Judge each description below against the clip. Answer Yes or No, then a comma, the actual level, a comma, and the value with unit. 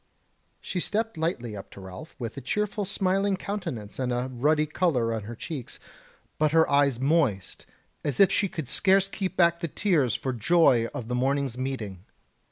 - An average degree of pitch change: No, wide, 6.7 semitones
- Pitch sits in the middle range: Yes, medium, 145 Hz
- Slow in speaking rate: No, average, 175 wpm